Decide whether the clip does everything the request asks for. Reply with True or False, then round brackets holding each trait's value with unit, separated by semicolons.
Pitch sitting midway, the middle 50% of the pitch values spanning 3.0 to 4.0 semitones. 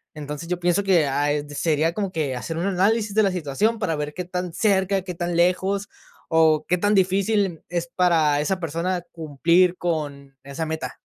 True (175 Hz; 3.6 semitones)